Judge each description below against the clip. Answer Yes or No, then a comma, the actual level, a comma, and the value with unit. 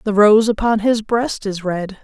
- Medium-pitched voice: No, high, 210 Hz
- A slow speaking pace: No, fast, 205 wpm